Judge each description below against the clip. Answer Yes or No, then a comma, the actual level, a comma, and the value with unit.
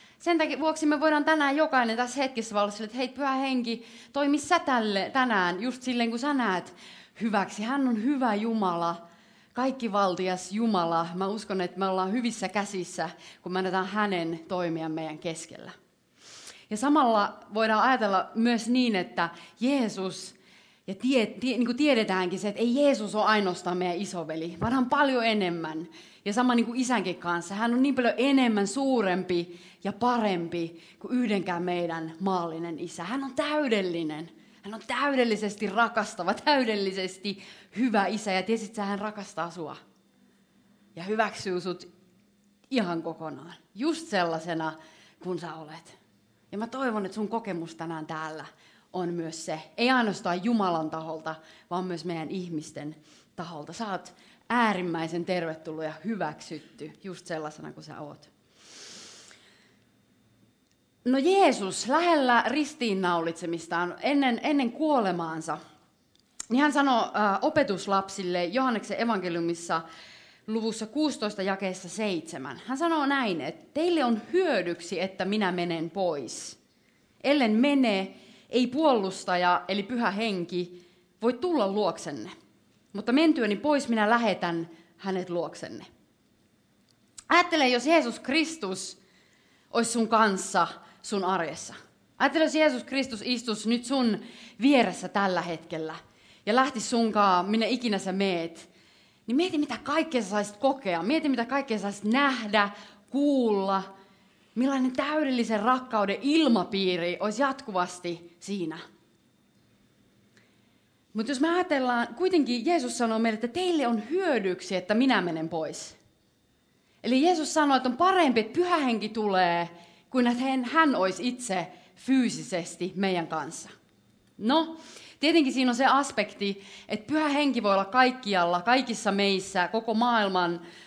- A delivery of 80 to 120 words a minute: No, average, 130 wpm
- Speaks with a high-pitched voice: Yes, high, 210 Hz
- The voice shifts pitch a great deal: Yes, wide, 5.9 semitones